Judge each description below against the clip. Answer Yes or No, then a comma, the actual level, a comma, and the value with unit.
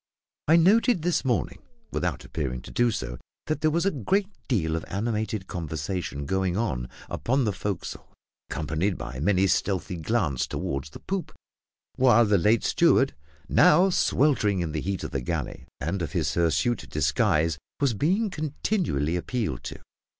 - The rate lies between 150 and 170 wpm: Yes, average, 155 wpm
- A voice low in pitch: Yes, low, 100 Hz